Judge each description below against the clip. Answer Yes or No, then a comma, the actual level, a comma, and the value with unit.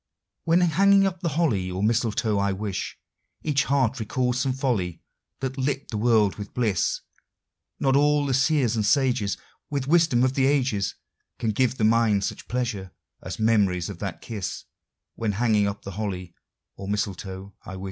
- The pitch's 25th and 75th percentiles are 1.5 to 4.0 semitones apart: No, average, 5.0 semitones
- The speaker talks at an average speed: Yes, average, 170 wpm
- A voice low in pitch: Yes, low, 115 Hz